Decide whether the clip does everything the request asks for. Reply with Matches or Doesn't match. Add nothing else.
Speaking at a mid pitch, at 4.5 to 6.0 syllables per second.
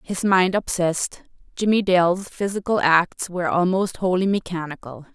Matches